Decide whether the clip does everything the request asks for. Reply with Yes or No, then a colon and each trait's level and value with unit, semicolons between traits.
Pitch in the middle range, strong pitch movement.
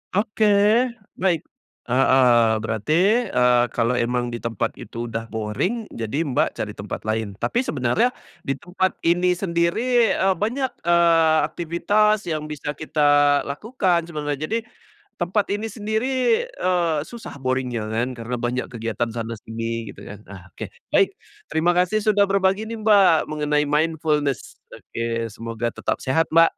Yes: medium, 155 Hz; wide, 8.5 semitones